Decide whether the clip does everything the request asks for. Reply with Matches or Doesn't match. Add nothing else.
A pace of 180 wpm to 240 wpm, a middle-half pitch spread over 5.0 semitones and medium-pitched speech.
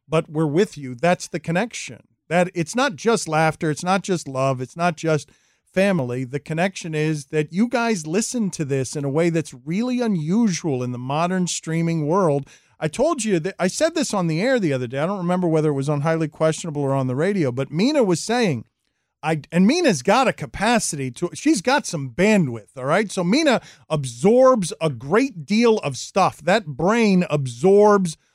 Matches